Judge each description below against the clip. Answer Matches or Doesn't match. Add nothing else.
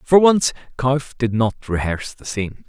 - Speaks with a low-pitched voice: Matches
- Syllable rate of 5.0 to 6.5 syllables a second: Doesn't match